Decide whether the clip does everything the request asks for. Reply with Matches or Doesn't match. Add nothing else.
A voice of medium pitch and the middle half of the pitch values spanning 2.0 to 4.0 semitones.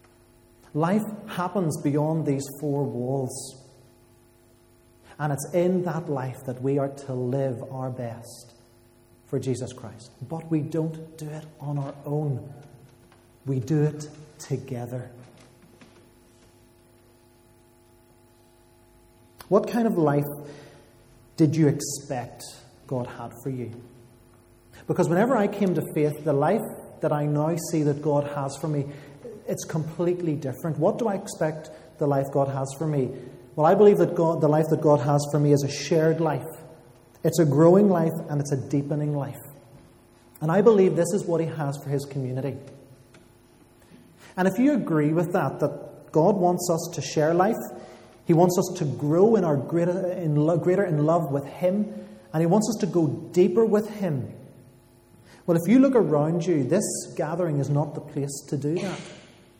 Doesn't match